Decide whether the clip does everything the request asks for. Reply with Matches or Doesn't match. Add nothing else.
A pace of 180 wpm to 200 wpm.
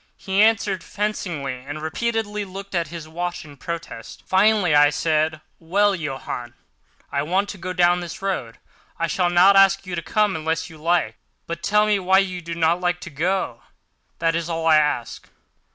Matches